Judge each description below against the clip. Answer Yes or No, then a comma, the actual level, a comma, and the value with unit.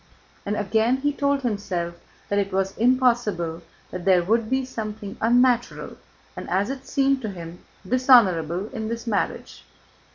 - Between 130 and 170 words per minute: Yes, average, 150 wpm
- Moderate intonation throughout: Yes, average, 4.8 semitones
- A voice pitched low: No, high, 220 Hz